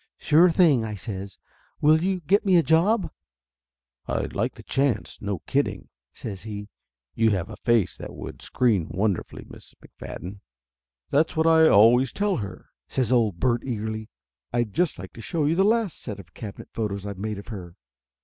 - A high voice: No, low, 115 Hz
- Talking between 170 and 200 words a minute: Yes, average, 180 wpm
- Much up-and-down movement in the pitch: Yes, wide, 7.9 semitones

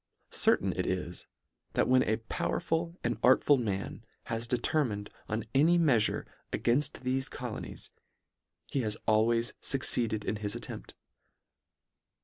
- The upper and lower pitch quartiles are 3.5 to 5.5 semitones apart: Yes, average, 4.0 semitones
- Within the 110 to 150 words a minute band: Yes, slow, 135 wpm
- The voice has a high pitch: No, low, 120 Hz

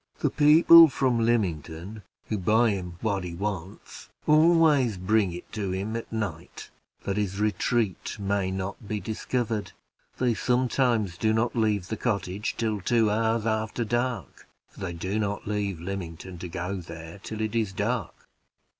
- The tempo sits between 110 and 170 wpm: Yes, average, 155 wpm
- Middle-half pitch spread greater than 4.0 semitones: No, average, 3.5 semitones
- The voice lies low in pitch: Yes, low, 105 Hz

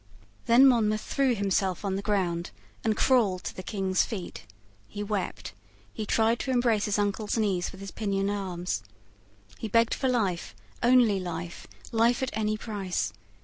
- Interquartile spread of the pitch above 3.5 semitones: No, average, 3.2 semitones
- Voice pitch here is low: No, high, 205 Hz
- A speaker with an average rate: Yes, average, 160 wpm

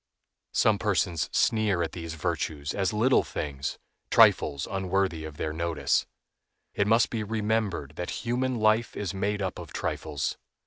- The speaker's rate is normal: Yes, average, 145 wpm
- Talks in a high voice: No, very low, 95 Hz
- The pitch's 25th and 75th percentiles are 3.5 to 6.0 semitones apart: Yes, average, 5.2 semitones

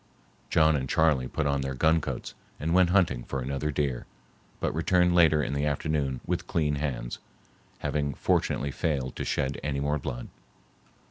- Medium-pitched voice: No, very low, 75 Hz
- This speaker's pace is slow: No, average, 165 wpm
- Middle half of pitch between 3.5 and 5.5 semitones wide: No, average, 2.8 semitones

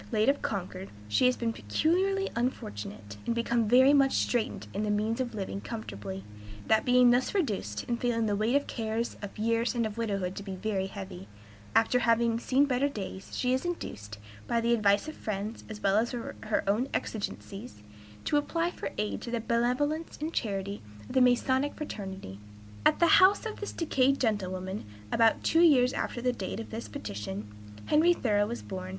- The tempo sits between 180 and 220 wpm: Yes, average, 185 wpm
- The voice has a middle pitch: No, high, 230 Hz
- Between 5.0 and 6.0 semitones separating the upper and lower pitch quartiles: No, average, 4.5 semitones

